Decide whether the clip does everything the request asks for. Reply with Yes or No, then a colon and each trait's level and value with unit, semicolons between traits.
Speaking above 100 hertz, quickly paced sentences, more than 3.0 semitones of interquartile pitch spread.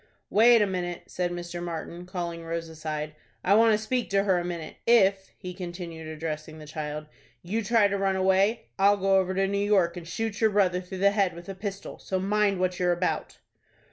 No: medium, 185 Hz; fast, 210 wpm; narrow, 2.6 semitones